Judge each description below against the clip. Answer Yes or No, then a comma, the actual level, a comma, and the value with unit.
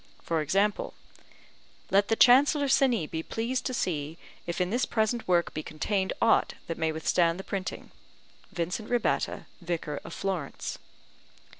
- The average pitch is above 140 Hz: Yes, high, 190 Hz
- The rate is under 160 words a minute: Yes, average, 145 wpm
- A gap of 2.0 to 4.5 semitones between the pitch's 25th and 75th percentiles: No, average, 5.3 semitones